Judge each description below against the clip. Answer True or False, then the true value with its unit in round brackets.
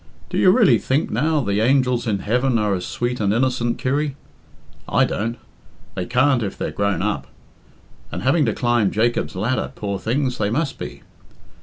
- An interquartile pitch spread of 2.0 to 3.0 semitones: False (4.0 semitones)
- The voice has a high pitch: False (120 Hz)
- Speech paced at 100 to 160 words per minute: False (175 wpm)